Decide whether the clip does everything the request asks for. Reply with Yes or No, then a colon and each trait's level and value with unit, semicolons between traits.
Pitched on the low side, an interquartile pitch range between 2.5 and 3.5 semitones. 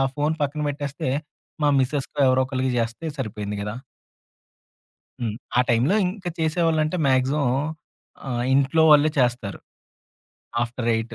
No: low, 130 Hz; average, 4.0 semitones